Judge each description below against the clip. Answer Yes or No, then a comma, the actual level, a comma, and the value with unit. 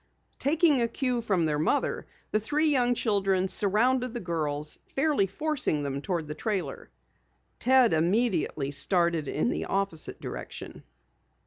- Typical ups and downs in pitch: No, wide, 7.4 semitones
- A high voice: Yes, high, 200 Hz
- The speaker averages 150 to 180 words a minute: No, slow, 135 wpm